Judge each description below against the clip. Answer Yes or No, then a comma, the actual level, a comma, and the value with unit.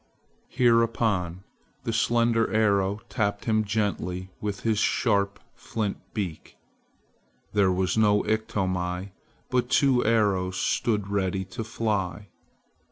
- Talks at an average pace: No, slow, 105 wpm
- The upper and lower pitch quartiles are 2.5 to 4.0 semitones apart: Yes, average, 3.0 semitones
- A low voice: Yes, low, 105 Hz